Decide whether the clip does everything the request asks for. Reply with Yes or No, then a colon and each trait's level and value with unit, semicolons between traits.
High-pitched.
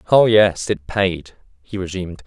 No: very low, 95 Hz